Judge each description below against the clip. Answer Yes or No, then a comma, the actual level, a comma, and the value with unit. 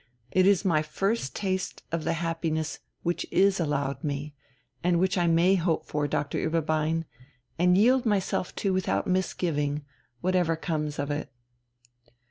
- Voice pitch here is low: No, medium, 165 Hz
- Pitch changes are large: No, average, 3.4 semitones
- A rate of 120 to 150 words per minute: Yes, average, 145 wpm